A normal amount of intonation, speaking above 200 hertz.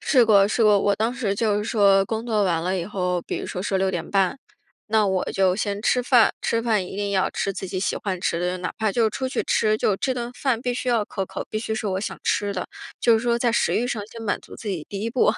Yes: average, 3.0 semitones; high, 210 Hz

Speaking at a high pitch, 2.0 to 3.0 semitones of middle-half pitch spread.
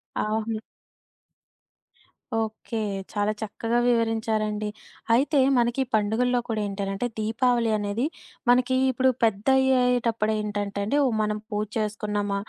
Yes: high, 220 Hz; narrow, 2.5 semitones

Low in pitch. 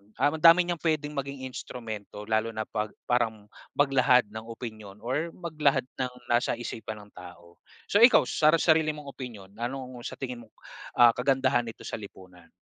Yes: low, 125 Hz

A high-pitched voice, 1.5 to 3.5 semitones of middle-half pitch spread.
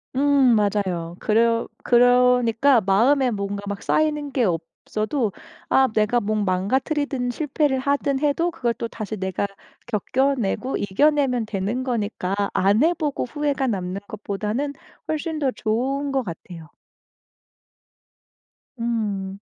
No: high, 235 Hz; average, 5.3 semitones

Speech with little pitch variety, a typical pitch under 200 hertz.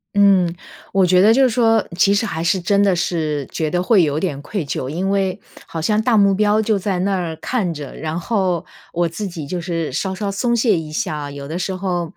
No: average, 3.7 semitones; medium, 185 Hz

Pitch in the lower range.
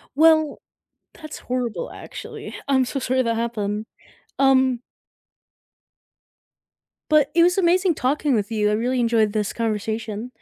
No: very high, 250 Hz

